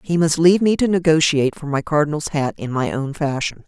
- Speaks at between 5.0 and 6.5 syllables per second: Yes, 5.9 syllables/s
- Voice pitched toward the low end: No, medium, 155 Hz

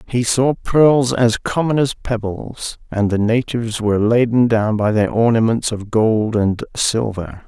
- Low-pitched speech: Yes, low, 115 Hz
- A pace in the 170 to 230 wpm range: No, average, 160 wpm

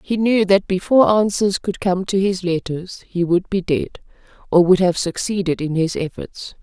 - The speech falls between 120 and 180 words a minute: No, average, 190 wpm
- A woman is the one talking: Yes, female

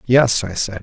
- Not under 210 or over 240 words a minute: Yes, fast, 220 wpm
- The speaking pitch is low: Yes, low, 110 Hz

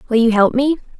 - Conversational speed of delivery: No, fast, 240 wpm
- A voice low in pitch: No, high, 245 Hz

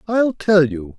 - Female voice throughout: No, male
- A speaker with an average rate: Yes, average, 185 wpm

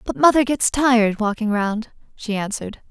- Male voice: No, female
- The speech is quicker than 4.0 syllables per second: Yes, 5.1 syllables/s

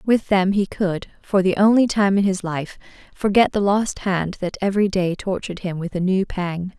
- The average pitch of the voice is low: No, high, 190 Hz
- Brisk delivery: Yes, fast, 210 wpm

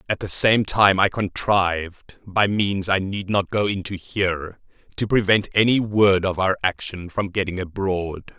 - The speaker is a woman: No, male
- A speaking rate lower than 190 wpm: Yes, average, 170 wpm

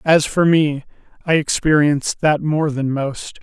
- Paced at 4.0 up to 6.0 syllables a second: Yes, 4.2 syllables/s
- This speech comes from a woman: No, male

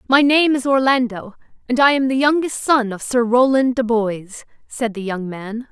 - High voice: Yes, high, 245 Hz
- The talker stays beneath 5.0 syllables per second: Yes, 4.7 syllables/s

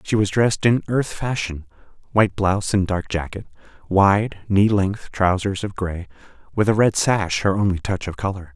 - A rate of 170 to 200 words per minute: Yes, average, 175 wpm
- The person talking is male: Yes, male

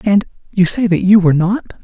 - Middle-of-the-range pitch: No, high, 195 Hz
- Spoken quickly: No, average, 195 wpm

